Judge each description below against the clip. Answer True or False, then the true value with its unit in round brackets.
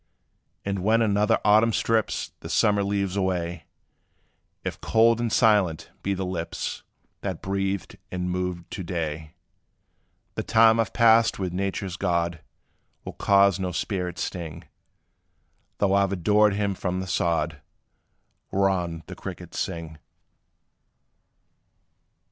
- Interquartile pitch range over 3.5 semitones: False (2.8 semitones)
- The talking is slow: True (125 wpm)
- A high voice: False (95 Hz)